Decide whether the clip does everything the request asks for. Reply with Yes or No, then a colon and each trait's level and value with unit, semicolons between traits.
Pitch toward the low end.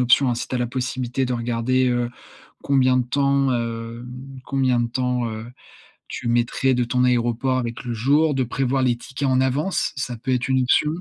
Yes: low, 125 Hz